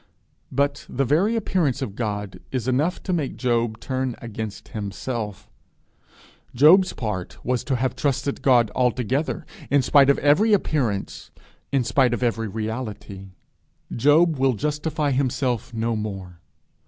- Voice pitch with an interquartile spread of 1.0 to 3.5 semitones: No, average, 4.4 semitones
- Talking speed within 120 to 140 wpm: Yes, slow, 135 wpm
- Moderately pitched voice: No, low, 125 Hz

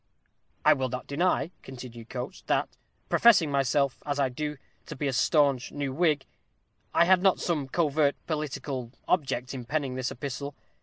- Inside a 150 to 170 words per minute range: Yes, average, 160 wpm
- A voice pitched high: No, medium, 140 Hz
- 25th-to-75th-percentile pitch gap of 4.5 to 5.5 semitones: No, average, 2.8 semitones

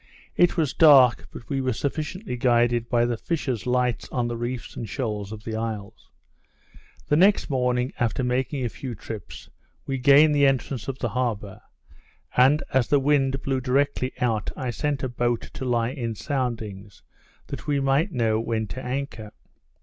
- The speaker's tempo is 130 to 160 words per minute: No, average, 175 wpm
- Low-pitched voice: Yes, low, 125 Hz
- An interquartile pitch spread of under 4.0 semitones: Yes, average, 3.0 semitones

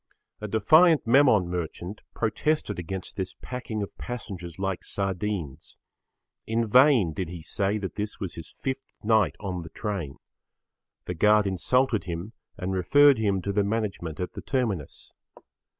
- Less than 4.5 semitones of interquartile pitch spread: Yes, average, 3.9 semitones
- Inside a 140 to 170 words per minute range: Yes, average, 150 wpm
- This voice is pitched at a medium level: No, low, 100 Hz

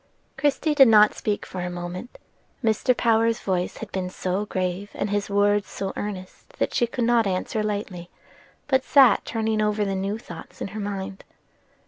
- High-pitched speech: Yes, high, 205 Hz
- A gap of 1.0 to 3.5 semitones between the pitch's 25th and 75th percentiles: Yes, average, 2.9 semitones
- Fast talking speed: No, average, 175 wpm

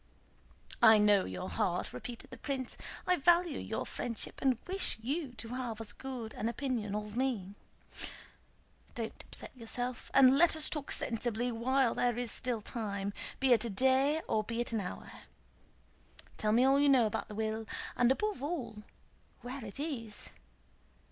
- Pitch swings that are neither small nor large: Yes, average, 3.4 semitones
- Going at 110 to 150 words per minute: No, average, 170 wpm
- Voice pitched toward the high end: Yes, high, 245 Hz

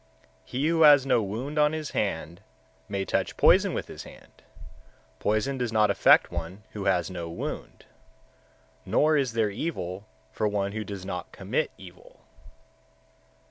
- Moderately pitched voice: No, low, 105 Hz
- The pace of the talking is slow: No, average, 155 wpm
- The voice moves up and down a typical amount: No, wide, 6.2 semitones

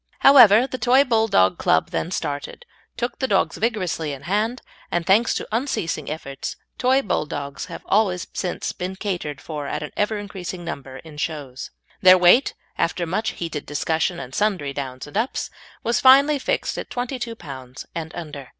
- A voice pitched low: No, medium, 180 Hz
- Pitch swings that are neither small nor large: No, wide, 7.3 semitones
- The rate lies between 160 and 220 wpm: Yes, average, 170 wpm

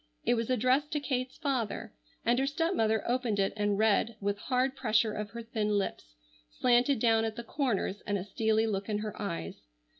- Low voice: No, high, 225 Hz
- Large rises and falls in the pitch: No, average, 3.4 semitones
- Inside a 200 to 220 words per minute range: No, average, 190 wpm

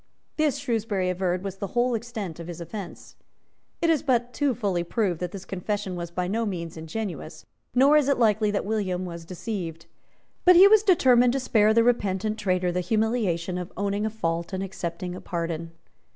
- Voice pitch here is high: Yes, high, 200 Hz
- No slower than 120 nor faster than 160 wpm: No, average, 190 wpm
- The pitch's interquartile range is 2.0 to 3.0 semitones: No, average, 4.7 semitones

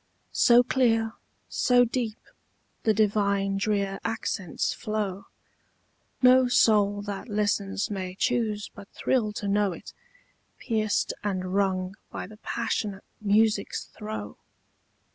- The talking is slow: Yes, slow, 110 wpm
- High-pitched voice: Yes, high, 210 Hz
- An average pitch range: No, narrow, 2.1 semitones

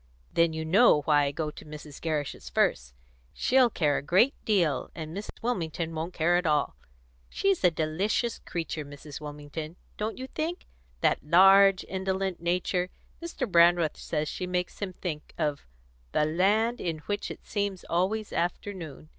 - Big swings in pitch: No, average, 4.2 semitones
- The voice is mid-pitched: Yes, medium, 175 Hz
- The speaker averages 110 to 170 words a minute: Yes, average, 160 wpm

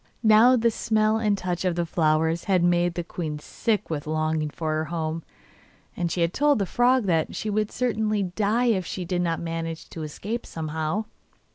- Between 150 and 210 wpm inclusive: Yes, average, 185 wpm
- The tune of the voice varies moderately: Yes, average, 4.8 semitones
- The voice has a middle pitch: Yes, medium, 175 Hz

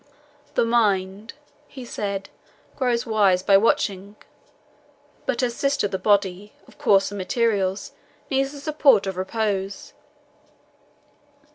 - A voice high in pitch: Yes, high, 205 Hz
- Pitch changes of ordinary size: Yes, average, 3.5 semitones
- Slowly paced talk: Yes, slow, 110 wpm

